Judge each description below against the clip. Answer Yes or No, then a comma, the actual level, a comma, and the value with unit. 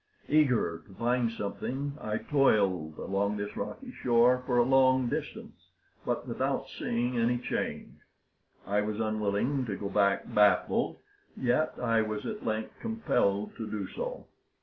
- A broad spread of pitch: No, average, 3.7 semitones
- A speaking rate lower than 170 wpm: Yes, average, 145 wpm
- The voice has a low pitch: Yes, low, 115 Hz